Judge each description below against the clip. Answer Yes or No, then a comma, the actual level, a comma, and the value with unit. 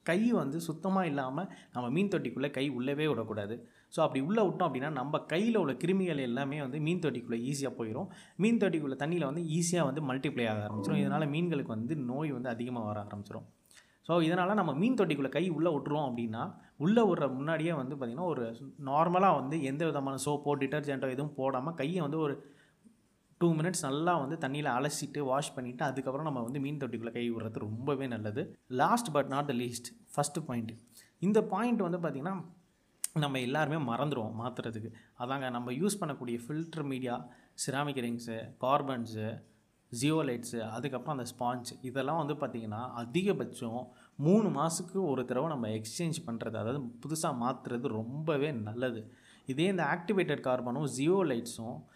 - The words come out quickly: Yes, fast, 155 wpm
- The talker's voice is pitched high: No, medium, 140 Hz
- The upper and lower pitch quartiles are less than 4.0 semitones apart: No, average, 5.2 semitones